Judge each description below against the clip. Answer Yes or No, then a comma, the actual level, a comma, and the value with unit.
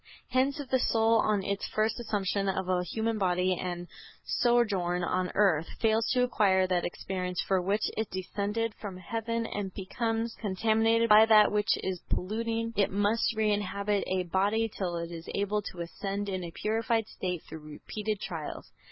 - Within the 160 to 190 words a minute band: Yes, average, 170 wpm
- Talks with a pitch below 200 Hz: No, high, 205 Hz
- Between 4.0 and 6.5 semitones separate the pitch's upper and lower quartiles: No, average, 3.3 semitones